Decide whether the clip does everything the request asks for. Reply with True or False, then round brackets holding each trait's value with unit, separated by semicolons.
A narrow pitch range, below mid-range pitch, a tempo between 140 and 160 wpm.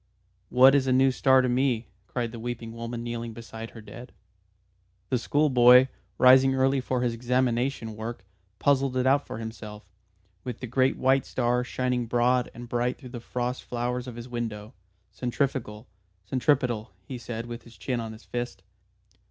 False (1.8 semitones; 120 Hz; 170 wpm)